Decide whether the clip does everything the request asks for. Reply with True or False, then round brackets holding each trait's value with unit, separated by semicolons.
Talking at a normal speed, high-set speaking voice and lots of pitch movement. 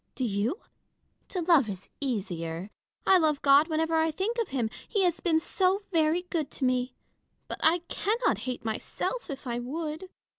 True (175 wpm; 310 Hz; 6.0 semitones)